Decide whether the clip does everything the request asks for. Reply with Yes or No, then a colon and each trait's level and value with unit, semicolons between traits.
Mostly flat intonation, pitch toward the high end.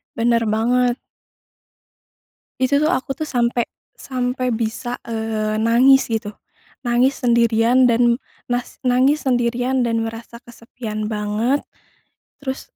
Yes: narrow, 2.0 semitones; high, 240 Hz